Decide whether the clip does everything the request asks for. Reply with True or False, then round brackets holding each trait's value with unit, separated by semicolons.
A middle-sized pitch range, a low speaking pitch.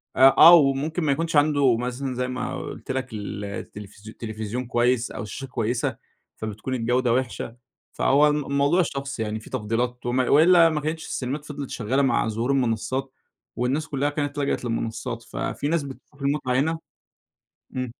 True (3.5 semitones; 130 Hz)